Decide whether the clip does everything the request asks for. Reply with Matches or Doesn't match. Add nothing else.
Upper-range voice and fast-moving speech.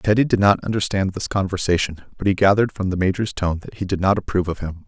Doesn't match